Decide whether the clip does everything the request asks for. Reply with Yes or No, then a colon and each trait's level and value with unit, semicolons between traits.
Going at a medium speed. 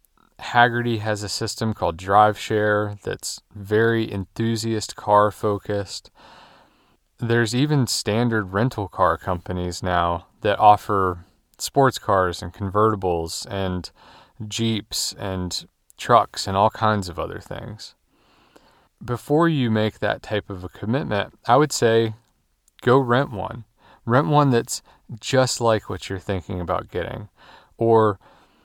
No: slow, 125 wpm